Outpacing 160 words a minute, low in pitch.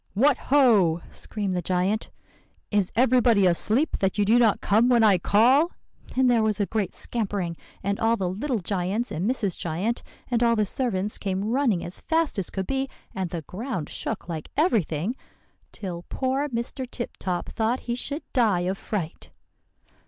No: average, 175 wpm; high, 215 Hz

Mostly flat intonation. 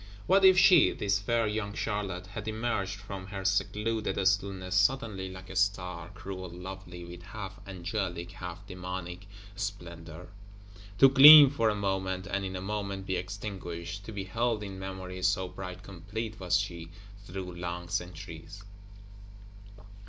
Yes: narrow, 2.1 semitones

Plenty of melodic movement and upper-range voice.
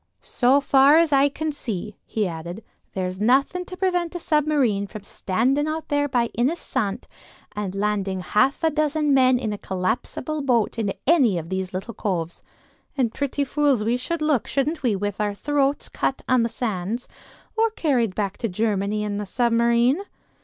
Yes: wide, 6.0 semitones; high, 240 Hz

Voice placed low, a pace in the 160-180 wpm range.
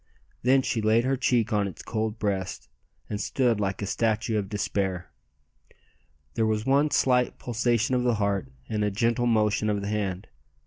Yes: low, 110 Hz; average, 175 wpm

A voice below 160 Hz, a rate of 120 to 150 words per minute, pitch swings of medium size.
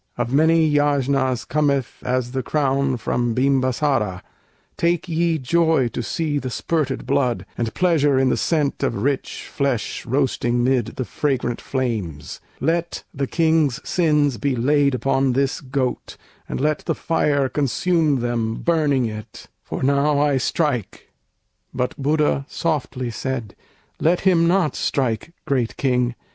Yes: low, 135 Hz; average, 140 wpm; average, 3.3 semitones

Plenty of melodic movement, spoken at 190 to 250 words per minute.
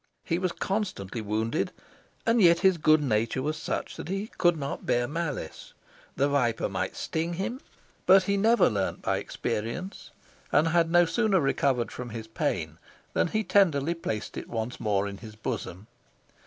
No: wide, 8.1 semitones; average, 170 wpm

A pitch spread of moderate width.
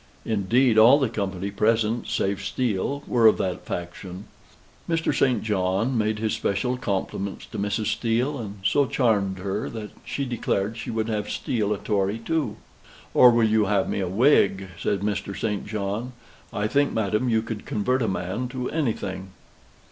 Yes: average, 3.4 semitones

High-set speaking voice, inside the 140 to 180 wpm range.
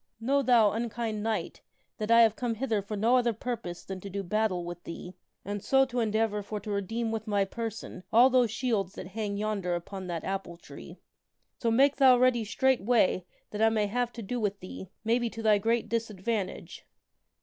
No: high, 220 Hz; average, 195 wpm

